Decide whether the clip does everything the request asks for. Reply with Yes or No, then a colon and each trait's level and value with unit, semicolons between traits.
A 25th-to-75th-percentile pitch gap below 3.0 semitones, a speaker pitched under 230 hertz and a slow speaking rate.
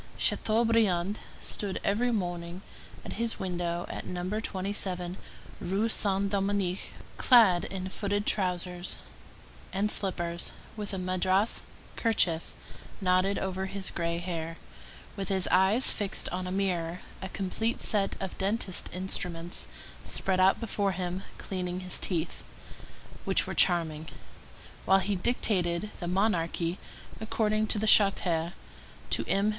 Yes: narrow, 2.4 semitones; high, 190 Hz; slow, 125 wpm